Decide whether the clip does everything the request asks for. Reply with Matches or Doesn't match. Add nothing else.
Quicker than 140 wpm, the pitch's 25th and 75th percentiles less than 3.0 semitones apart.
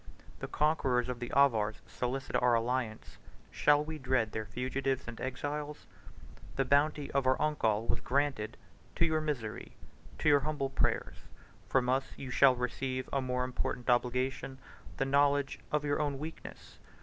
Matches